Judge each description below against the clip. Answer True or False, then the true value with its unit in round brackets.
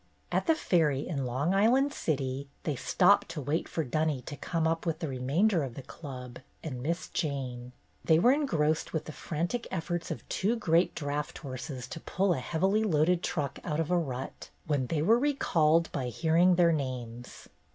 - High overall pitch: False (160 Hz)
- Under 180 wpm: False (190 wpm)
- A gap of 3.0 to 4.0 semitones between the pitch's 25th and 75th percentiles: False (4.5 semitones)